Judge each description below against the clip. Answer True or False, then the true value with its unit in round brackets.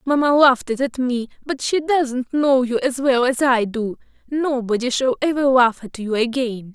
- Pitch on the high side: True (255 Hz)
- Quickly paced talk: False (185 wpm)